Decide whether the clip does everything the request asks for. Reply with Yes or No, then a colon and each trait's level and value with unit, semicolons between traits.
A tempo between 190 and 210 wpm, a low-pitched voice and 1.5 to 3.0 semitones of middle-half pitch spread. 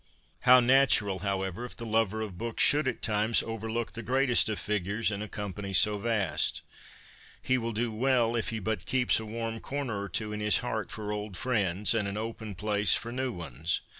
Yes: average, 200 wpm; low, 110 Hz; narrow, 2.5 semitones